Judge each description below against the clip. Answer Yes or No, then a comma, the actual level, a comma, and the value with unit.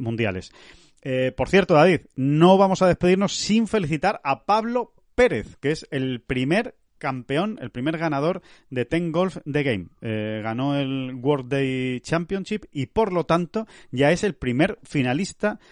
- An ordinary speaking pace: Yes, average, 160 wpm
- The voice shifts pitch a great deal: Yes, wide, 6.4 semitones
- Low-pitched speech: No, medium, 155 Hz